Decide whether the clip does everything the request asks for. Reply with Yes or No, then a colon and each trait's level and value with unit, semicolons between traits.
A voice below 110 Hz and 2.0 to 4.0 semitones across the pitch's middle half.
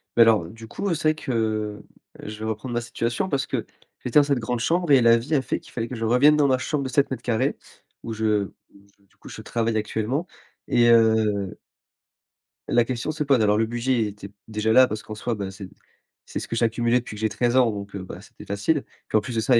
No: low, 115 Hz; average, 3.1 semitones